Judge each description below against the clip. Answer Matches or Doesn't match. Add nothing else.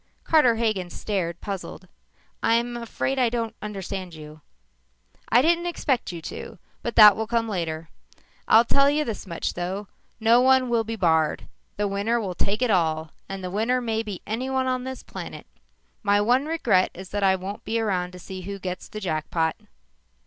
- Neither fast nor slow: Matches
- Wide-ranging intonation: Doesn't match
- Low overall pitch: Doesn't match